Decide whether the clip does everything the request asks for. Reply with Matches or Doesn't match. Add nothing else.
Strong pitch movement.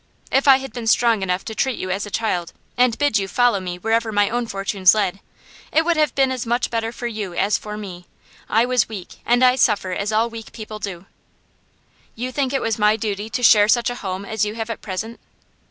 Doesn't match